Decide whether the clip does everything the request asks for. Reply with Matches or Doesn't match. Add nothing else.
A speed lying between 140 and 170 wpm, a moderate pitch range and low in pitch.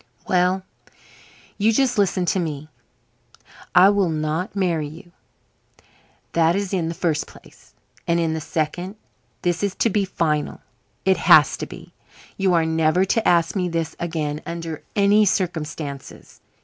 Doesn't match